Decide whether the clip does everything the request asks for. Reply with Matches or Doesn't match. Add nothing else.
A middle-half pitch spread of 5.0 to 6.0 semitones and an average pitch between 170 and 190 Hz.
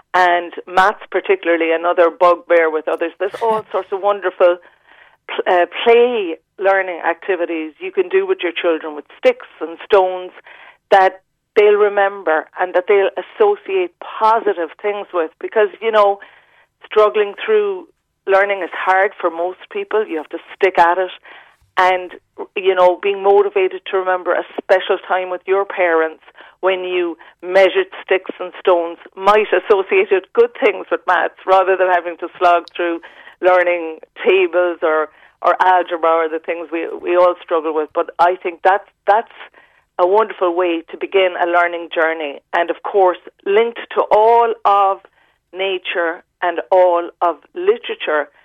Doesn't match